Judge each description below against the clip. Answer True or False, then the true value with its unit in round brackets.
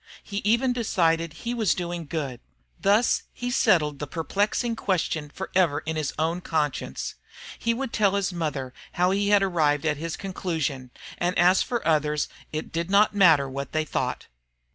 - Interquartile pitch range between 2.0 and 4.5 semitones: False (4.9 semitones)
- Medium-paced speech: True (165 wpm)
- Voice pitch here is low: False (170 Hz)